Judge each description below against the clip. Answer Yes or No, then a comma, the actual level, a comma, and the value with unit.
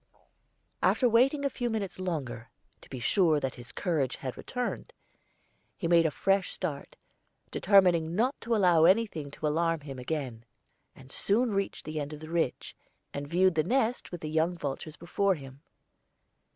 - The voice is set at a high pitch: No, medium, 165 Hz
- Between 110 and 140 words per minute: No, average, 165 wpm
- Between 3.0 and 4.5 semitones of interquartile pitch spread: No, wide, 5.4 semitones